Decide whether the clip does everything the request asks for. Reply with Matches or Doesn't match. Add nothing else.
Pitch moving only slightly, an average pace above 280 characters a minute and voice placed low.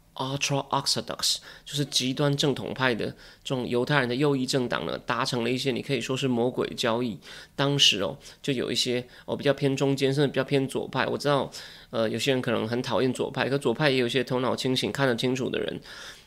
Matches